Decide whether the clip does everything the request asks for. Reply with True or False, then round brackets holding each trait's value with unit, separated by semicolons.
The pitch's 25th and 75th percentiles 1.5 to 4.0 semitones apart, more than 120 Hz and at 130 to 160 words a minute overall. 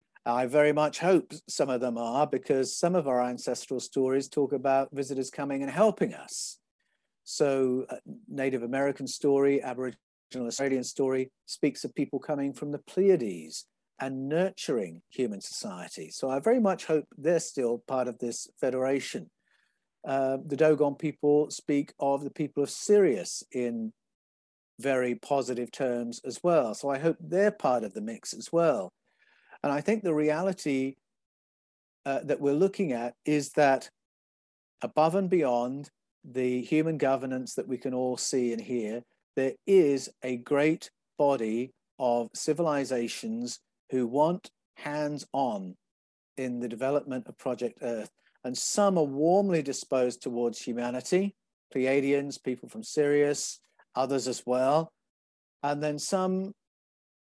True (3.3 semitones; 135 Hz; 140 wpm)